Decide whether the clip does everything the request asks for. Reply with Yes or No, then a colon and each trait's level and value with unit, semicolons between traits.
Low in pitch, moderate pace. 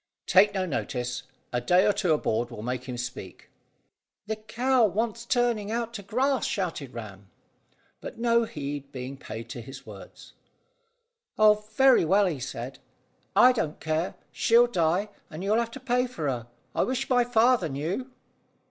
No: high, 190 Hz; average, 165 wpm